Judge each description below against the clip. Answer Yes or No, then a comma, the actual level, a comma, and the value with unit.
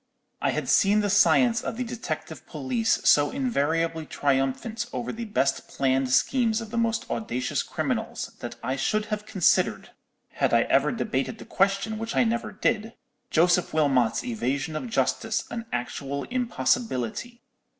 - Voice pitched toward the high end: Yes, high, 205 Hz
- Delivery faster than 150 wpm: No, average, 145 wpm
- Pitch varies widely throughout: Yes, wide, 8.6 semitones